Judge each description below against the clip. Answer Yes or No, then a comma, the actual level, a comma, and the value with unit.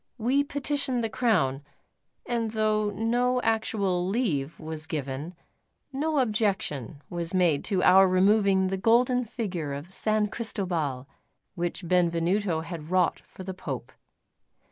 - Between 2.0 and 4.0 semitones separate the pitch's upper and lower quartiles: No, average, 5.1 semitones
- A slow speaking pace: Yes, slow, 125 wpm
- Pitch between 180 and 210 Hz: Yes, high, 190 Hz